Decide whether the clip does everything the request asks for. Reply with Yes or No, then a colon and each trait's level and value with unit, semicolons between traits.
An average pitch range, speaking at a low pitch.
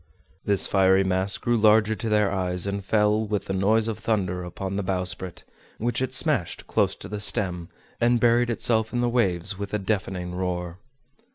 Yes: average, 3.1 semitones; low, 100 Hz